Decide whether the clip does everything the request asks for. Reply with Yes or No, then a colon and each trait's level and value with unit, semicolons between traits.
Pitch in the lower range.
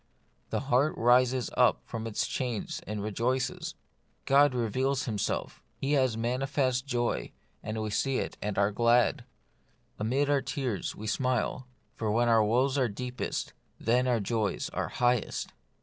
Yes: low, 125 Hz